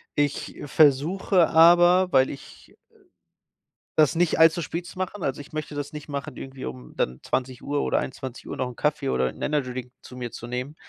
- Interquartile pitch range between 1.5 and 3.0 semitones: No, average, 3.9 semitones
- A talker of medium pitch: Yes, medium, 145 Hz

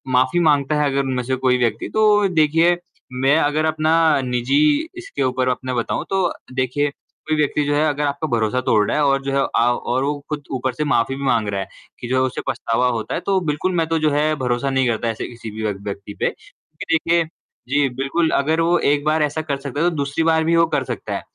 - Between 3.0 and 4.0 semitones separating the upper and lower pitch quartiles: Yes, average, 3.7 semitones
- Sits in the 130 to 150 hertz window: Yes, medium, 140 Hz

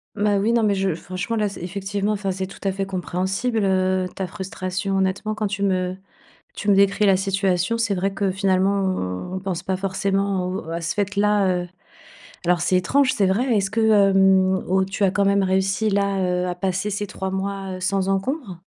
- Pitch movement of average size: No, narrow, 1.3 semitones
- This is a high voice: Yes, high, 195 Hz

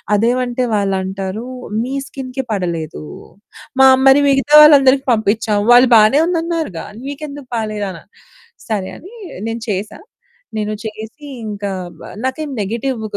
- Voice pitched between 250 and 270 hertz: No, high, 230 Hz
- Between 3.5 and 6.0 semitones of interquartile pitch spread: Yes, average, 4.8 semitones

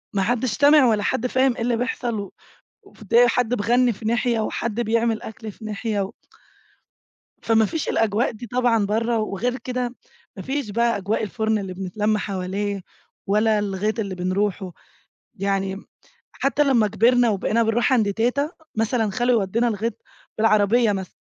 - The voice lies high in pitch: Yes, high, 220 Hz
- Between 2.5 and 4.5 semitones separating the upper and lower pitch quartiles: Yes, average, 3.0 semitones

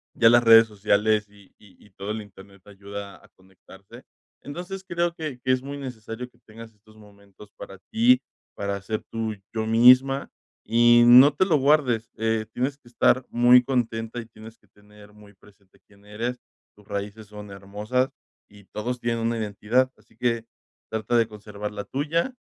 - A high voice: No, low, 115 Hz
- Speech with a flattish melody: No, average, 3.3 semitones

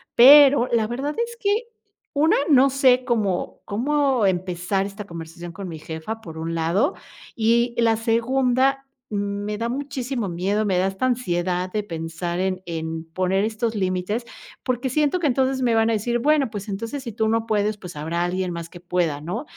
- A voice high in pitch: Yes, high, 215 Hz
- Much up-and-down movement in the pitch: Yes, wide, 5.8 semitones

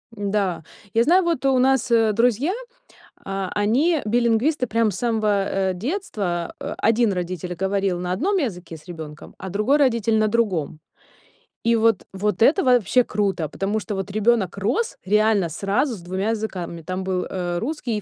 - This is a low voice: No, high, 210 Hz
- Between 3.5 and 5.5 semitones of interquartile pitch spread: Yes, average, 4.0 semitones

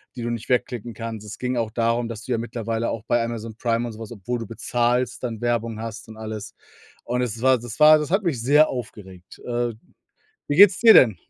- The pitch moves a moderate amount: No, narrow, 1.8 semitones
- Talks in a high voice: No, low, 115 Hz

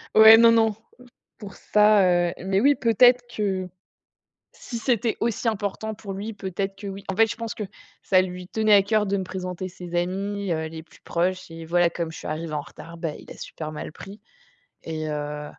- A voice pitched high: Yes, high, 195 Hz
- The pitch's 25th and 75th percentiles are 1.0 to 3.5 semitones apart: No, average, 4.0 semitones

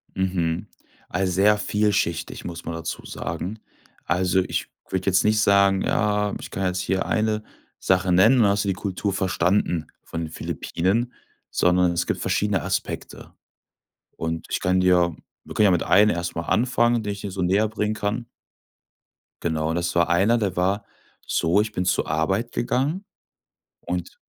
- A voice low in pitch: Yes, very low, 95 Hz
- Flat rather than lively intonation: No, average, 3.1 semitones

